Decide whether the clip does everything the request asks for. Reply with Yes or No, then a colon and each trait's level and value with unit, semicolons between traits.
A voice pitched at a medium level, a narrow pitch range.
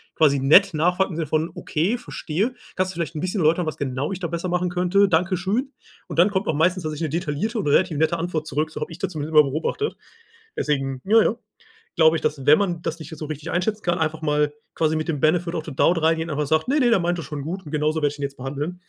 No: medium, 165 Hz; average, 3.0 semitones